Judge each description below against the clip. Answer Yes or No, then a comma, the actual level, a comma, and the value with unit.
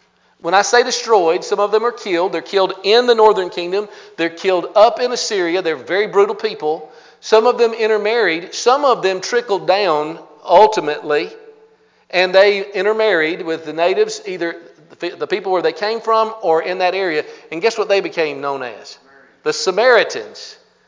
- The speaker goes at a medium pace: Yes, average, 170 wpm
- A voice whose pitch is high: Yes, high, 200 Hz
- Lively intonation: Yes, wide, 5.8 semitones